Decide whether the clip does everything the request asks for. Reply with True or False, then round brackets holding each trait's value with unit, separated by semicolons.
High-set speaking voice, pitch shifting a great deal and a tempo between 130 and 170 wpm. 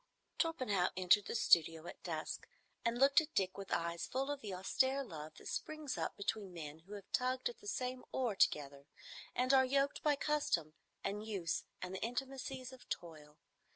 False (210 Hz; 7.5 semitones; 185 wpm)